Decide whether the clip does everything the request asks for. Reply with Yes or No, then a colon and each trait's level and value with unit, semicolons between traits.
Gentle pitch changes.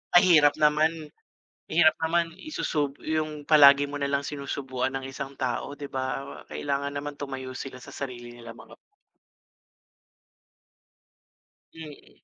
Yes: narrow, 2.3 semitones